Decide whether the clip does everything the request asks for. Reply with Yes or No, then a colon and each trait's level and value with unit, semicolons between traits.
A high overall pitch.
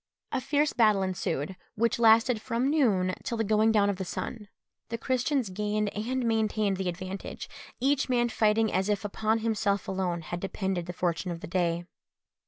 Yes: high, 210 Hz